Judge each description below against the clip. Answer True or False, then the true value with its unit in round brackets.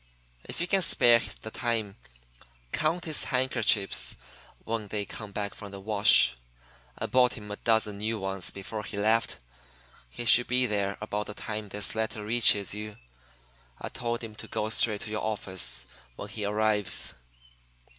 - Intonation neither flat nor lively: False (2.1 semitones)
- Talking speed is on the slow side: False (165 wpm)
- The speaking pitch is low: True (105 Hz)